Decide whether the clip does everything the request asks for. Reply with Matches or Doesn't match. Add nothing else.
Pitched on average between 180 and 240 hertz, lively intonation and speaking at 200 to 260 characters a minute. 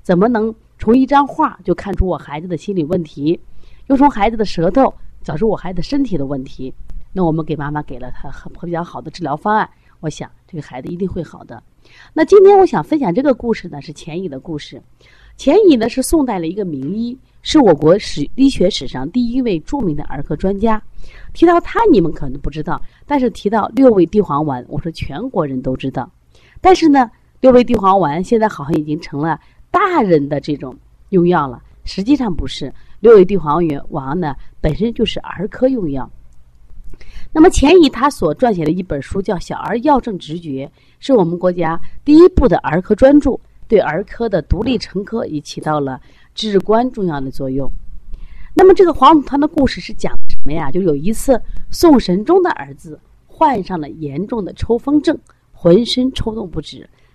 Doesn't match